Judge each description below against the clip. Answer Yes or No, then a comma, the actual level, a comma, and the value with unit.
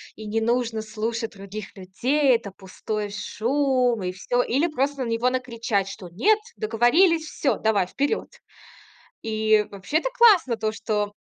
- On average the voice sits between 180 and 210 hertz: No, high, 225 Hz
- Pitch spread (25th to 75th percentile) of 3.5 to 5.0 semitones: Yes, average, 4.0 semitones